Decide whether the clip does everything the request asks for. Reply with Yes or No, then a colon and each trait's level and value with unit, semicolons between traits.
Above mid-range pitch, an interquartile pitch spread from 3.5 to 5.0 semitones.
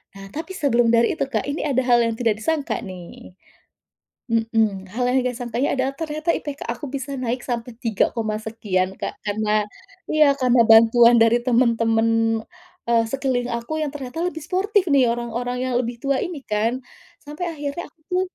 Yes: high, 245 Hz; average, 3.8 semitones